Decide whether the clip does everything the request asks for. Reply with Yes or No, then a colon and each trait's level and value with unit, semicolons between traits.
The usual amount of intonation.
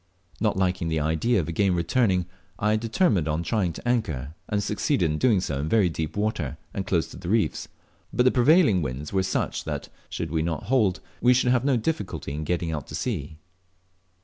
No: wide, 6.1 semitones